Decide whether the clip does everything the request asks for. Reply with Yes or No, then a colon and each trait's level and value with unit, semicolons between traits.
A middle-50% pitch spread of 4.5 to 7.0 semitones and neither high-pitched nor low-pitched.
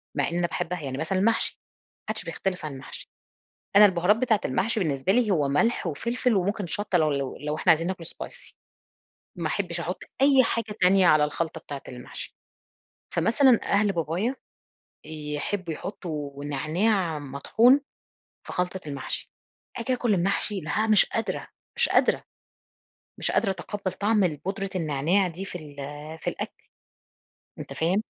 Yes: average, 5.2 semitones; medium, 180 Hz